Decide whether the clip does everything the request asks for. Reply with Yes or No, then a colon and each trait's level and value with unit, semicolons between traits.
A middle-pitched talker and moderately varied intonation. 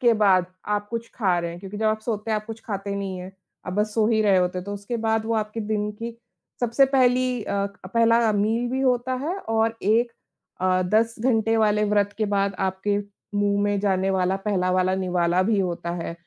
No: high, 210 Hz; average, 3.0 semitones